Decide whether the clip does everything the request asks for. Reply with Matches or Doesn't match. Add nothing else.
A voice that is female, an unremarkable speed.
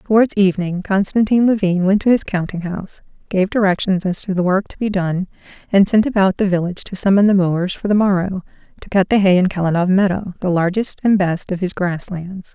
Doesn't match